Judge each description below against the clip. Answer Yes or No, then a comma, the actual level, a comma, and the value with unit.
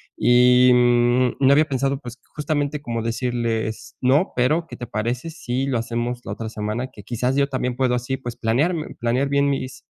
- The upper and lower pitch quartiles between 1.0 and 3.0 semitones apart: Yes, narrow, 2.5 semitones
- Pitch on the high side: No, low, 125 Hz